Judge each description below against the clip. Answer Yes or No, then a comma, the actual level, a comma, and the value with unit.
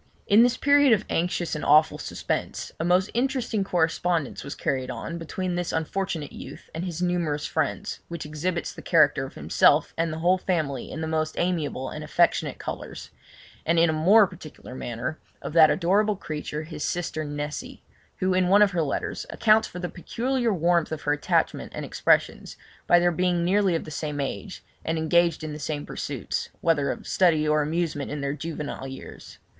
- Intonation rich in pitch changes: No, average, 3.1 semitones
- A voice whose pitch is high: No, medium, 165 Hz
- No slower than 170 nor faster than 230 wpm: Yes, average, 185 wpm